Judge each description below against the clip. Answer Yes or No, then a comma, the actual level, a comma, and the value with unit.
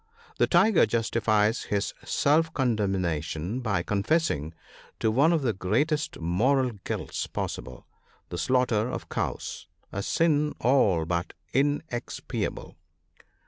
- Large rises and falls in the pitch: Yes, wide, 7.4 semitones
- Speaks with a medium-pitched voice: No, low, 115 Hz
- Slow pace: Yes, slow, 125 wpm